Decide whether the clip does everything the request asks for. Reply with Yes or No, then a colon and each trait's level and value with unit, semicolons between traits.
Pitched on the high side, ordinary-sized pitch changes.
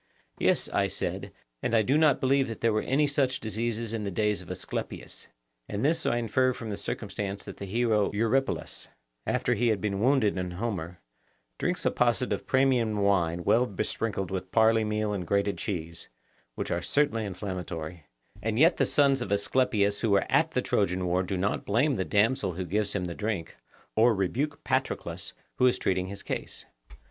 No: low, 105 Hz; average, 4.0 semitones